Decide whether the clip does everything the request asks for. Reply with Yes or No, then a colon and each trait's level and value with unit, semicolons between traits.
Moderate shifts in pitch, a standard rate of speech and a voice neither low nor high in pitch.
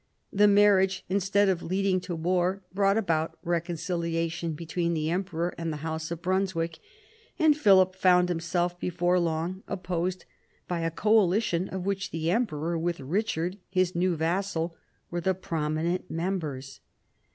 No: narrow, 2.3 semitones; average, 145 wpm; medium, 175 Hz